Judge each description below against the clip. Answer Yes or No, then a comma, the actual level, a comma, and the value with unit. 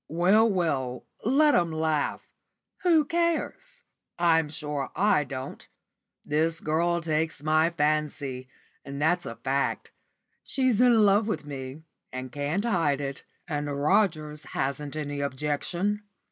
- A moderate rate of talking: No, slow, 125 wpm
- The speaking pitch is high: No, medium, 155 Hz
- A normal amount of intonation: Yes, average, 4.8 semitones